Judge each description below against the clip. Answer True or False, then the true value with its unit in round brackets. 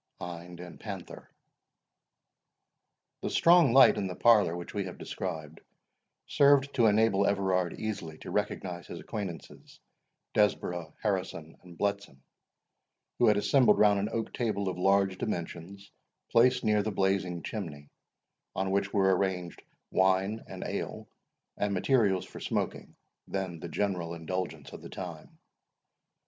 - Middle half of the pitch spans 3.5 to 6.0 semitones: False (3.1 semitones)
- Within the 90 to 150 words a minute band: True (135 wpm)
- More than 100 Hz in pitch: False (95 Hz)